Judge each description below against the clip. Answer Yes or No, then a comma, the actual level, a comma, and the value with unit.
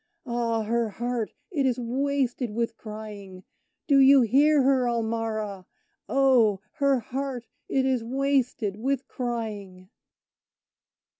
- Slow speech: Yes, slow, 115 wpm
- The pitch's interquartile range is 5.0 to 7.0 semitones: No, average, 3.5 semitones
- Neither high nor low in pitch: No, high, 240 Hz